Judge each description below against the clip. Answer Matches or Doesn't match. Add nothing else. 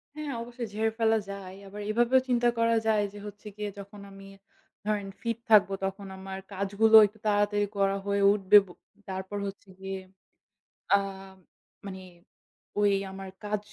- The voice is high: Matches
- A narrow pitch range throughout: Matches